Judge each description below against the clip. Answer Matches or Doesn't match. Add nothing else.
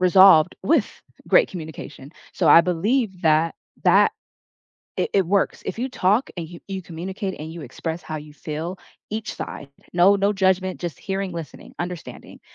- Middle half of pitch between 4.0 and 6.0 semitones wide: Doesn't match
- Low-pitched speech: Doesn't match